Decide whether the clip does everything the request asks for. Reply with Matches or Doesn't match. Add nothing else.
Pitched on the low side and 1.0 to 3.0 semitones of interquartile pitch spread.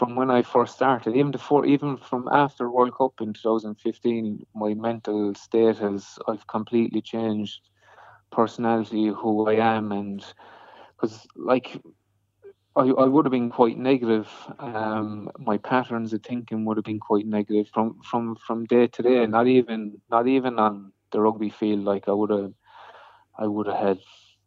Matches